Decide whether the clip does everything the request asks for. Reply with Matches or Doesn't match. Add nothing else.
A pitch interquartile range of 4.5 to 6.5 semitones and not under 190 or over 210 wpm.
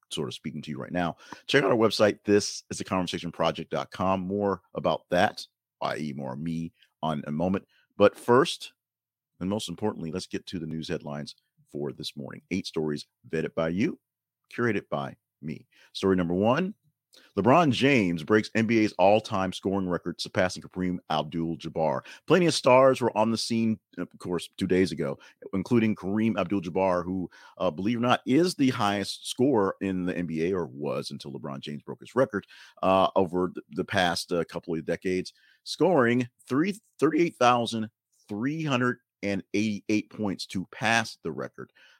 Doesn't match